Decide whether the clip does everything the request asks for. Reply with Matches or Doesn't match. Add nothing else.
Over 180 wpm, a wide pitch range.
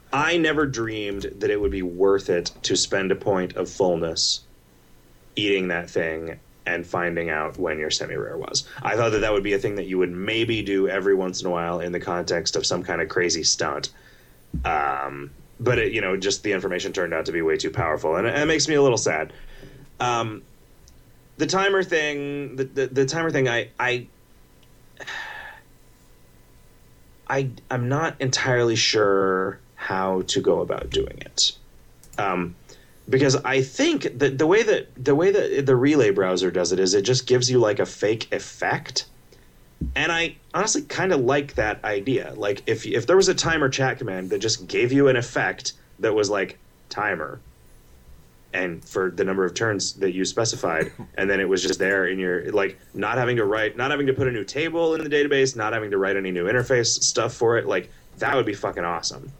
Matches